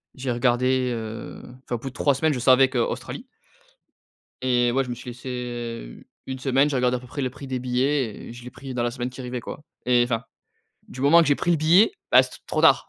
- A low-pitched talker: Yes, low, 125 Hz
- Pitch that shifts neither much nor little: No, narrow, 1.8 semitones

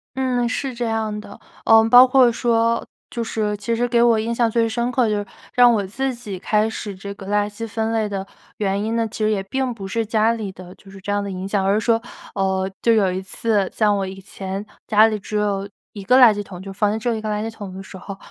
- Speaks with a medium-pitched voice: No, high, 215 Hz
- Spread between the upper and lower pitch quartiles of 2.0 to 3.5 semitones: Yes, narrow, 2.6 semitones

